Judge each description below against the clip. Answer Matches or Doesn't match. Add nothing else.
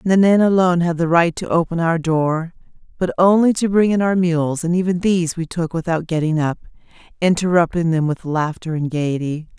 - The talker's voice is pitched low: Doesn't match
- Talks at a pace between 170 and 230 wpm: Matches